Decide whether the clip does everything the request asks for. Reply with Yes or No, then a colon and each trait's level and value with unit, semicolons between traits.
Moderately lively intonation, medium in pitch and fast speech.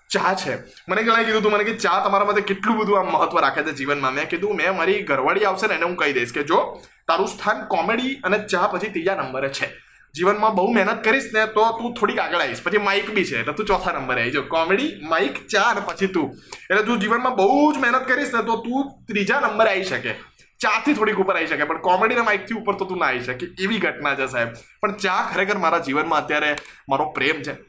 No: average, 5.0 semitones; high, 200 Hz; fast, 240 wpm